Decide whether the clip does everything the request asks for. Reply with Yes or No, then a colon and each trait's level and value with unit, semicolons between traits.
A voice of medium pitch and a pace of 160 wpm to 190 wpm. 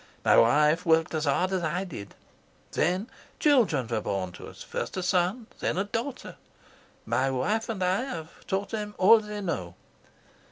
Yes: medium, 180 Hz; average, 175 wpm